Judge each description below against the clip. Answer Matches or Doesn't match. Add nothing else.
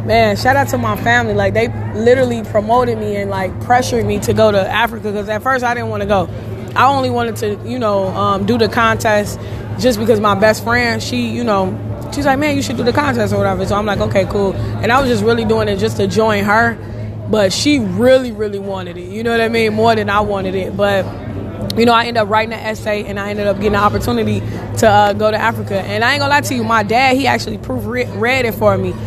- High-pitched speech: Matches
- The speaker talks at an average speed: Doesn't match